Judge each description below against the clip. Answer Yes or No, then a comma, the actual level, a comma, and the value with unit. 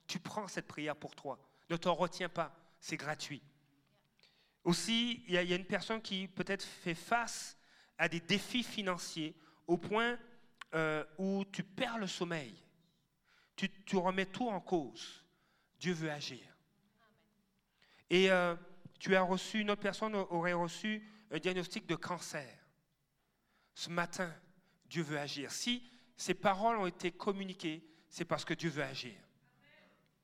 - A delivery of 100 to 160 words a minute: Yes, average, 150 wpm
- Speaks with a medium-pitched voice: Yes, medium, 180 Hz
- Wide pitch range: No, average, 3.5 semitones